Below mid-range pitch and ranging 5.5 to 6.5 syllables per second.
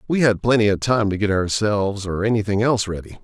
Yes: low, 105 Hz; 6.2 syllables/s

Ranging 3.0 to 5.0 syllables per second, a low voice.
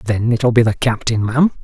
No: 5.3 syllables/s; low, 120 Hz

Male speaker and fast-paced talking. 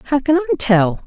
No: female; fast, 225 wpm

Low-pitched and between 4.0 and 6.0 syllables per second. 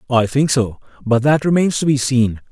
Yes: low, 130 Hz; 5.0 syllables/s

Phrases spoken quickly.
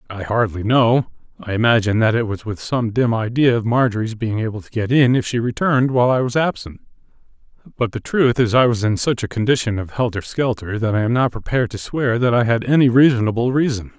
Yes: fast, 215 wpm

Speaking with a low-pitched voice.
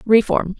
No: high, 215 Hz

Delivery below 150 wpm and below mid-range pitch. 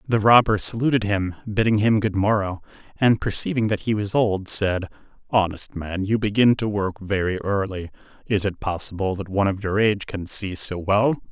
No: average, 185 wpm; low, 100 Hz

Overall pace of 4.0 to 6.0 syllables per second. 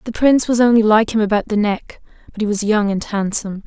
No: 6.2 syllables/s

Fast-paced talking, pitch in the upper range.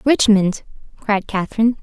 No: slow, 100 wpm; high, 215 Hz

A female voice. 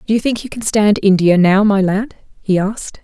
Yes: female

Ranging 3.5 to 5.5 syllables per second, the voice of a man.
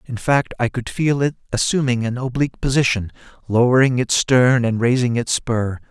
Yes: 5.1 syllables/s; male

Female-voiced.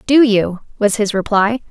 Yes: female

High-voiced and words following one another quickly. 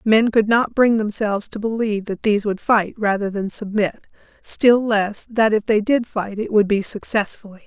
No: high, 215 Hz; average, 195 wpm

